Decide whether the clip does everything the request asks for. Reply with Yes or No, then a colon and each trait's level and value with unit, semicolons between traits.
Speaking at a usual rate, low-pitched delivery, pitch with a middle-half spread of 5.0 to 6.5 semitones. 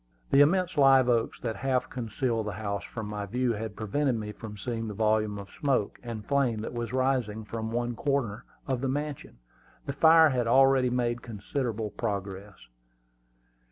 No: average, 170 wpm; low, 120 Hz; average, 3.7 semitones